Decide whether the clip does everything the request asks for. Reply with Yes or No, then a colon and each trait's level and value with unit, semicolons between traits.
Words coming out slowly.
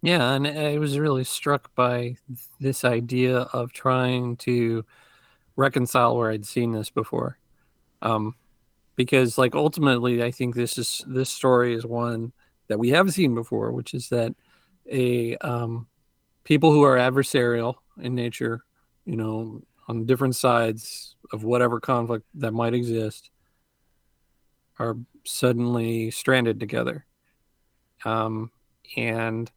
Yes: slow, 130 wpm